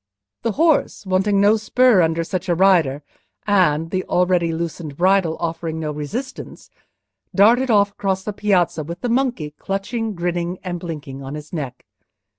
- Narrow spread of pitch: No, average, 4.0 semitones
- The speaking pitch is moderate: Yes, medium, 180 Hz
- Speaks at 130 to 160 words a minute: Yes, average, 155 wpm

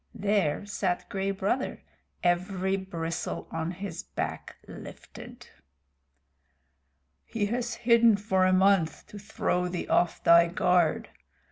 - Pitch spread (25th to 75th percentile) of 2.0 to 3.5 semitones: Yes, narrow, 2.5 semitones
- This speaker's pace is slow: Yes, slow, 115 wpm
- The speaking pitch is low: No, high, 190 Hz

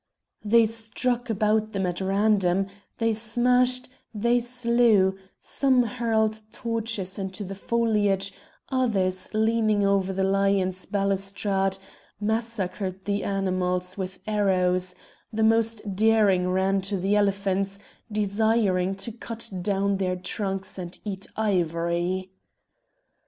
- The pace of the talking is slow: Yes, slow, 110 wpm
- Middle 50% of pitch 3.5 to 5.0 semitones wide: No, average, 2.8 semitones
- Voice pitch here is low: No, high, 200 Hz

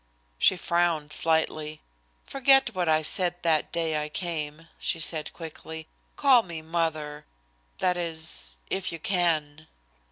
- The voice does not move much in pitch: Yes, narrow, 2.2 semitones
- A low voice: No, medium, 160 Hz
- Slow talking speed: Yes, slow, 130 wpm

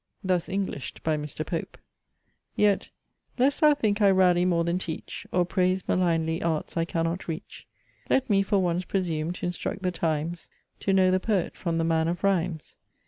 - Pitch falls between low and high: Yes, medium, 180 Hz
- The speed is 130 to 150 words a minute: No, average, 175 wpm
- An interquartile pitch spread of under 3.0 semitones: Yes, narrow, 2.6 semitones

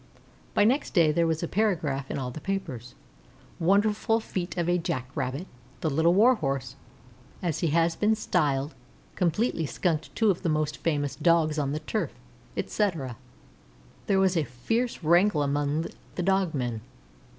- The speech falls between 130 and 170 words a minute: Yes, average, 150 wpm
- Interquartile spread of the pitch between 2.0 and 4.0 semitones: No, average, 4.9 semitones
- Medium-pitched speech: Yes, medium, 165 Hz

